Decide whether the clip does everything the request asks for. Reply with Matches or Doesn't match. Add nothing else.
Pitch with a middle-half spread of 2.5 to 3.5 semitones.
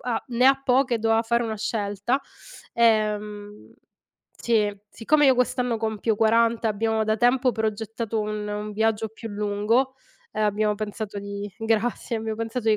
Doesn't match